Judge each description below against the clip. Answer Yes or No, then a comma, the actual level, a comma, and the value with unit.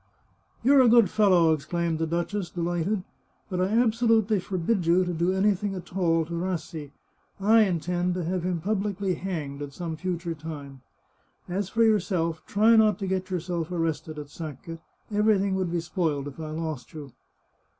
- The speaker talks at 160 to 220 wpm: Yes, average, 180 wpm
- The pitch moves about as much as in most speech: Yes, average, 3.5 semitones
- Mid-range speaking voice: Yes, medium, 180 Hz